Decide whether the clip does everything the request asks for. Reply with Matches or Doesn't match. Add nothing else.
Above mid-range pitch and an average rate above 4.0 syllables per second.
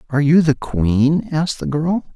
Doesn't match